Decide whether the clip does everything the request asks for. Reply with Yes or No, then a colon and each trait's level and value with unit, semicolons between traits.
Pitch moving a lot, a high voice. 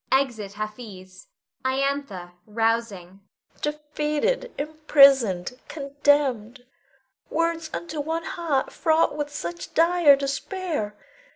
Yes: wide, 6.0 semitones; very high, 275 Hz